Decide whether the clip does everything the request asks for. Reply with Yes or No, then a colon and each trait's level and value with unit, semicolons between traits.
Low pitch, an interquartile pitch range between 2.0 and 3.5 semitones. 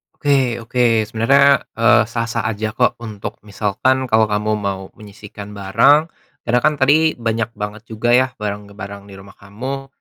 No: low, 115 Hz; average, 3.9 semitones